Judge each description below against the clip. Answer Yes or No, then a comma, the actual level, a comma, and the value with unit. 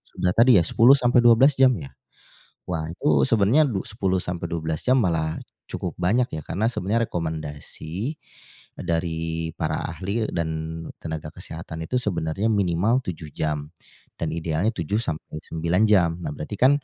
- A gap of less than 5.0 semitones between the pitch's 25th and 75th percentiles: No, wide, 5.6 semitones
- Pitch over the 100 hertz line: No, very low, 85 Hz